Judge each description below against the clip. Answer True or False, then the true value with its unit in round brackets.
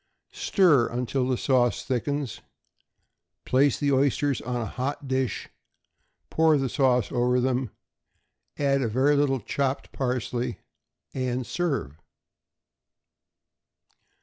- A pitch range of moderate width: False (2.3 semitones)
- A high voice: False (130 Hz)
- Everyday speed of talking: False (105 wpm)